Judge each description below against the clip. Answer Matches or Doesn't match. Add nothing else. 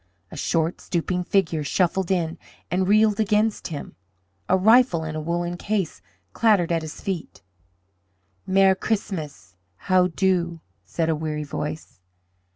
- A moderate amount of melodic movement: Matches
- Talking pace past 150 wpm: Doesn't match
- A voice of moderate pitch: Matches